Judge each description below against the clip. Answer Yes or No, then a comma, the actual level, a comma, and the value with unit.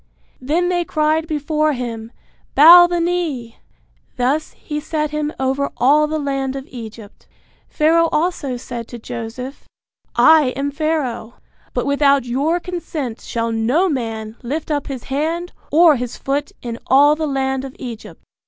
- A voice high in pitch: Yes, very high, 280 Hz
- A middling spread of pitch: Yes, average, 3.9 semitones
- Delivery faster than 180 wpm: No, average, 150 wpm